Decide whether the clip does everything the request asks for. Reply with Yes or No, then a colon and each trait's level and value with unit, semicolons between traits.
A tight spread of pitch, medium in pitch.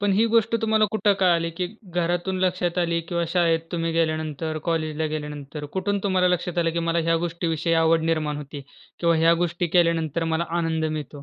Yes: narrow, 1.7 semitones; medium, 165 Hz